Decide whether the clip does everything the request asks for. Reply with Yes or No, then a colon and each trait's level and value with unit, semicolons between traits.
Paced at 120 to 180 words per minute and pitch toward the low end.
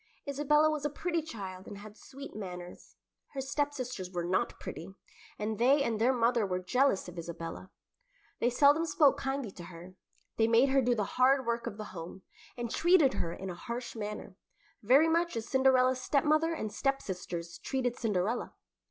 No: average, 175 wpm; high, 235 Hz